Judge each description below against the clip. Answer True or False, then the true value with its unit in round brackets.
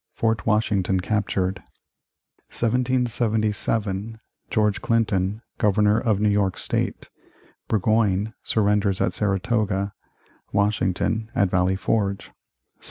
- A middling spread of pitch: False (2.2 semitones)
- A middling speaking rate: False (95 wpm)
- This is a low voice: True (105 Hz)